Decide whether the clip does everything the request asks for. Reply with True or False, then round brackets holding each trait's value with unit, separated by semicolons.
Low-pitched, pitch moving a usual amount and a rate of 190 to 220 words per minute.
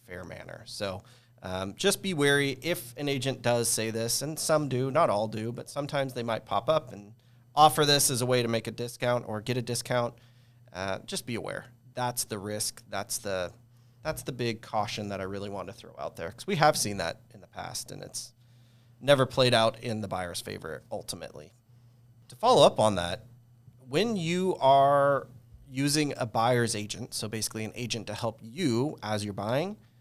True (120 Hz; 3.1 semitones; 200 wpm)